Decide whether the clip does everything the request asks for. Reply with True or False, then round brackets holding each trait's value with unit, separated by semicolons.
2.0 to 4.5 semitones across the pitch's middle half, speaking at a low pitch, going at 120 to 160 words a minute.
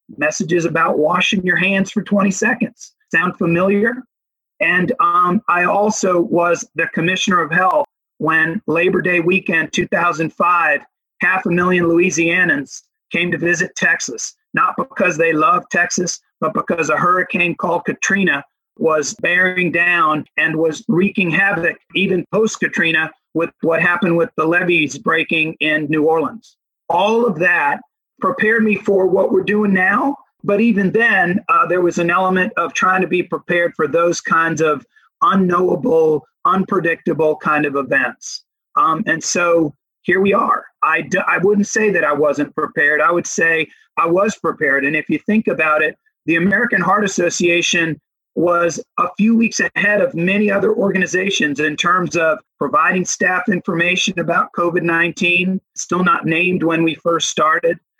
False (3.5 semitones; 180 Hz; 155 wpm)